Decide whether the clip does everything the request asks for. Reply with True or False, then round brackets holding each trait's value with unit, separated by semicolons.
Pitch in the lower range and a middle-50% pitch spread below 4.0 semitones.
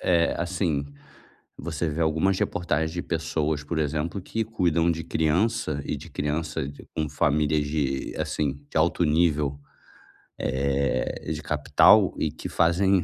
True (80 Hz; 2.5 semitones)